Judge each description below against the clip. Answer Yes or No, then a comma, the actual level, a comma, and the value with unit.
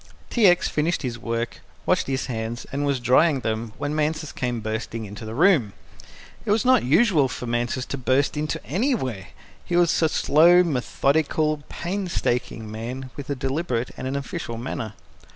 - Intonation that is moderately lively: Yes, average, 5.0 semitones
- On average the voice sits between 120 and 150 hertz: Yes, low, 135 Hz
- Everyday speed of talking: Yes, average, 170 wpm